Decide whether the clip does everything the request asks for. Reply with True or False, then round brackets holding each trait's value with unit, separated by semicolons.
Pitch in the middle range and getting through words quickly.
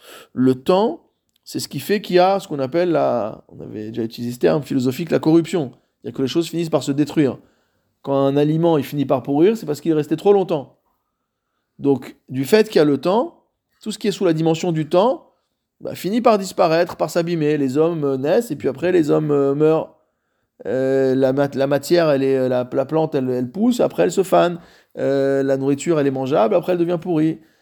True (150 Hz; 230 wpm)